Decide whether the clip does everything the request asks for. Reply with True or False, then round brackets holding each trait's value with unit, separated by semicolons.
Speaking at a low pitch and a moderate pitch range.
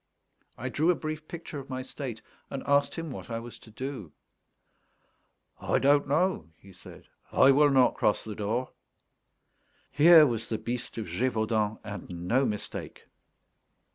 True (130 Hz; 4.7 semitones)